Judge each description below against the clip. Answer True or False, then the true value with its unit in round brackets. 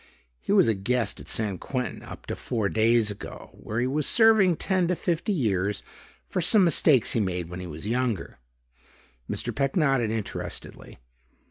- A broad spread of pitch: True (7.0 semitones)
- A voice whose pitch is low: True (120 Hz)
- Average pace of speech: True (170 wpm)